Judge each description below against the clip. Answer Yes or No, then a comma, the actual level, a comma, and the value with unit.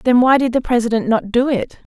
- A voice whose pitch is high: Yes, high, 240 Hz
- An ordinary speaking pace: No, fast, 245 wpm